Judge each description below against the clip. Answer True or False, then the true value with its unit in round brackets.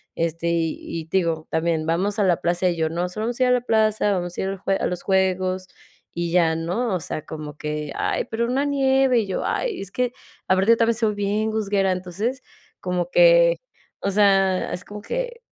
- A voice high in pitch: True (195 Hz)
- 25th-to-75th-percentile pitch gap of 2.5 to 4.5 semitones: False (4.9 semitones)